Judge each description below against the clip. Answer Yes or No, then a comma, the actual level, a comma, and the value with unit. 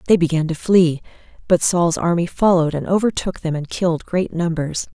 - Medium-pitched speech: Yes, medium, 170 Hz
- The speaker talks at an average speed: Yes, average, 180 wpm